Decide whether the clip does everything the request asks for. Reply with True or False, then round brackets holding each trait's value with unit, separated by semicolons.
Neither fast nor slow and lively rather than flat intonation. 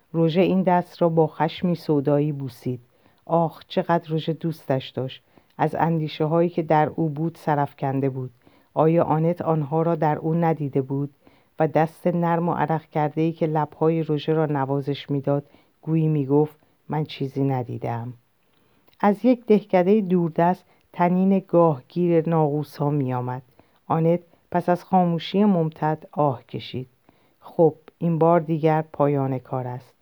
False (140 wpm; 3.0 semitones)